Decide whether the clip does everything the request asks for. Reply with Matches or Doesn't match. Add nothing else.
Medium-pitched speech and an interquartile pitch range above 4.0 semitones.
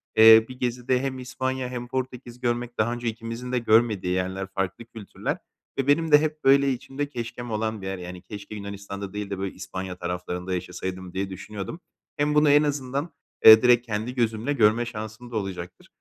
Doesn't match